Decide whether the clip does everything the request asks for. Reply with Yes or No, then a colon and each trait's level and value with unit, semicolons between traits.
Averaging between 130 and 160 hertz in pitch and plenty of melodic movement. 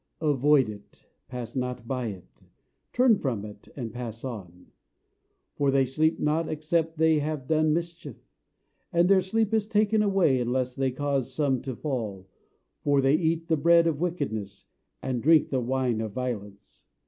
No: medium, 140 Hz; average, 4.8 semitones